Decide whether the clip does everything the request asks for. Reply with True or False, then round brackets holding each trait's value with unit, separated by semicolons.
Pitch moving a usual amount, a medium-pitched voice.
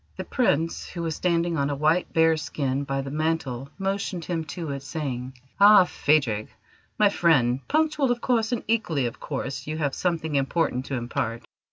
True (4.6 semitones; 155 Hz)